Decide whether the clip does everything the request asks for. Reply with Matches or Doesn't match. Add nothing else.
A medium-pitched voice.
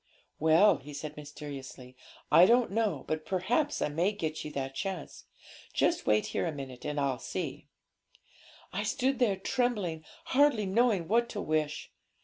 Matches